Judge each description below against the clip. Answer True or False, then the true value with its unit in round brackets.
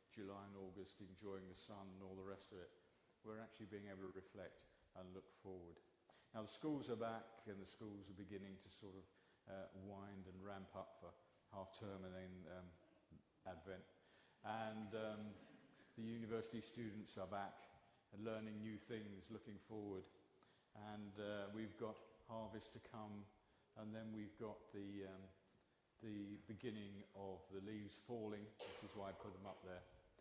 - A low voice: True (100 Hz)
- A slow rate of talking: False (170 wpm)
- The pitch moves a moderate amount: False (2.2 semitones)